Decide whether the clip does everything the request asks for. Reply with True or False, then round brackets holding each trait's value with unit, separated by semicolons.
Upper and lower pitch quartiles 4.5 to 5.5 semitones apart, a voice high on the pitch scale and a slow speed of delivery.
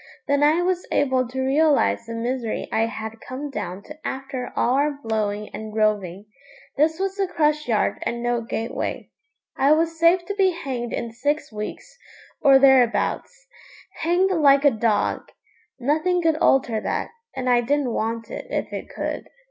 False (5.1 semitones; 265 Hz; 165 wpm)